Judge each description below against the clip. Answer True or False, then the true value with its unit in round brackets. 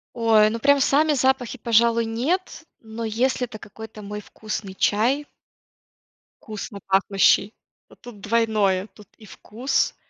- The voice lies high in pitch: True (225 Hz)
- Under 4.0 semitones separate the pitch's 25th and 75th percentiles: True (2.9 semitones)